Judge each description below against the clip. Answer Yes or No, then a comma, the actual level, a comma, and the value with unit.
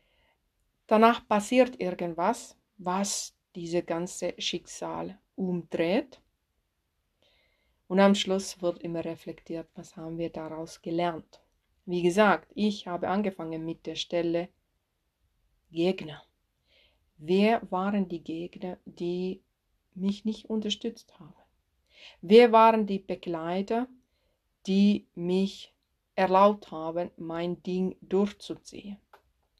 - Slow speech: Yes, slow, 95 wpm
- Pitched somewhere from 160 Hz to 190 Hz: Yes, medium, 185 Hz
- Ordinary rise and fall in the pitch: Yes, average, 3.3 semitones